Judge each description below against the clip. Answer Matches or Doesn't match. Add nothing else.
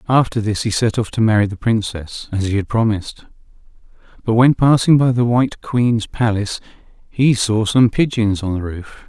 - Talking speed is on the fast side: Doesn't match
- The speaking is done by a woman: Doesn't match